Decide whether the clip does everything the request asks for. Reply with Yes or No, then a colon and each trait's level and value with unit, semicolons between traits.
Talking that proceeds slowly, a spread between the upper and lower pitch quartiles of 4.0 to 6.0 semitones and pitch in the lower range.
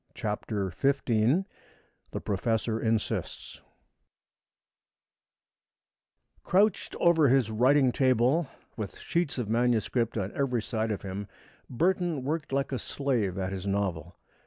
Yes: slow, 110 wpm; average, 4.9 semitones; low, 120 Hz